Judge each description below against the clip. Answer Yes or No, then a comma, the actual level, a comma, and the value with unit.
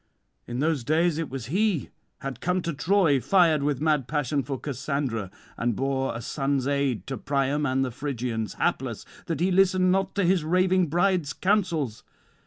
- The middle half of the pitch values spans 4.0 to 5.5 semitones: Yes, average, 4.9 semitones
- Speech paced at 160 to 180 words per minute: Yes, average, 175 wpm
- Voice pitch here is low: No, medium, 145 Hz